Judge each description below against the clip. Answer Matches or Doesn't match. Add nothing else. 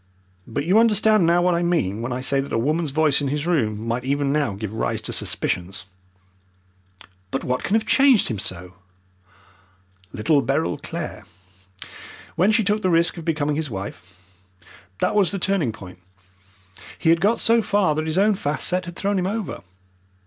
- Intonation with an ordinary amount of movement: Doesn't match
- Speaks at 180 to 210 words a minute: Matches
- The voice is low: Doesn't match